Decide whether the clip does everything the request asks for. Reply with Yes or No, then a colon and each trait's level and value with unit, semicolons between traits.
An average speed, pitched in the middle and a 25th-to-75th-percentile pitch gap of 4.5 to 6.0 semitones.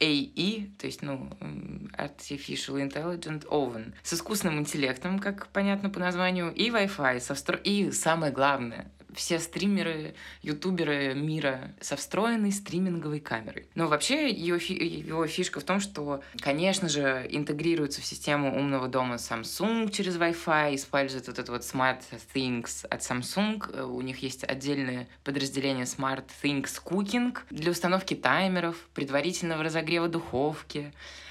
Yes: average, 135 wpm; medium, 150 Hz; average, 4.8 semitones